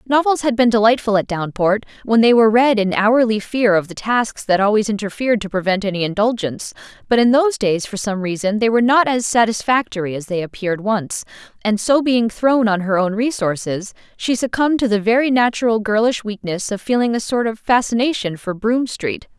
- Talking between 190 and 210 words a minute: Yes, average, 200 wpm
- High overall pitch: Yes, high, 220 Hz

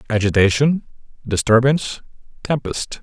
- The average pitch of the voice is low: Yes, low, 120 Hz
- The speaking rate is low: Yes, slow, 60 wpm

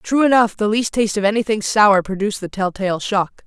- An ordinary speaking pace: No, fast, 225 wpm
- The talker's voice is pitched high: Yes, high, 210 Hz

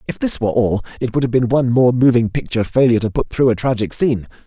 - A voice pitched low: Yes, low, 120 Hz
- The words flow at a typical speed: No, fast, 255 wpm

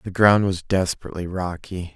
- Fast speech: No, average, 155 wpm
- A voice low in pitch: Yes, very low, 95 Hz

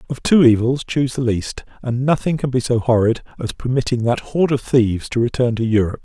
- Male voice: Yes, male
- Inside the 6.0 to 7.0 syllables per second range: Yes, 6.1 syllables/s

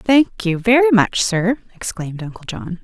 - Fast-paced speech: No, average, 170 wpm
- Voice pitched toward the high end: Yes, high, 205 Hz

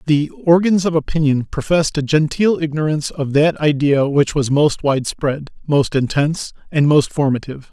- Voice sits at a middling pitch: Yes, medium, 150 Hz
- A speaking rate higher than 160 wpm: No, average, 155 wpm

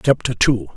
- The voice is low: Yes, low, 125 Hz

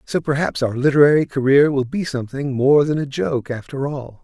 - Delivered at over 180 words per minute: Yes, average, 200 wpm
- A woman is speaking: No, male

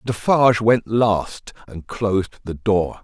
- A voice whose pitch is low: Yes, low, 105 Hz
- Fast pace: No, average, 140 wpm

